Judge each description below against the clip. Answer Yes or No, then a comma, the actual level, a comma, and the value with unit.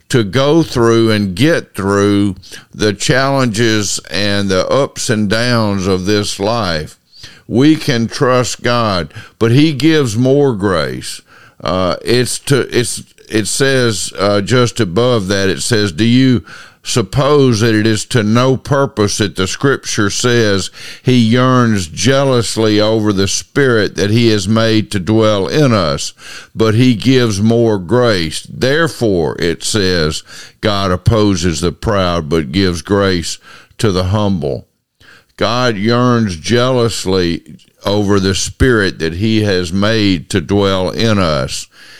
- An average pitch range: Yes, average, 3.7 semitones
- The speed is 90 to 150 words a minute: Yes, slow, 135 wpm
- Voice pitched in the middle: No, low, 110 Hz